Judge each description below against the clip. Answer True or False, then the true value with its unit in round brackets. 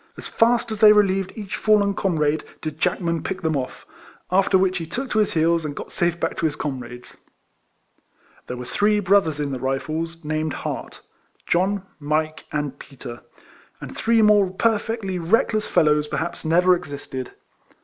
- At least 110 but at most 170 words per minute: False (180 wpm)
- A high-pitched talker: False (170 Hz)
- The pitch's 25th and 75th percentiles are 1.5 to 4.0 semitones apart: False (5.0 semitones)